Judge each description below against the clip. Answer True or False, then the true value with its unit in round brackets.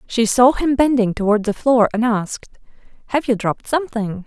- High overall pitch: True (235 Hz)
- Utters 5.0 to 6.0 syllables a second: True (5.5 syllables/s)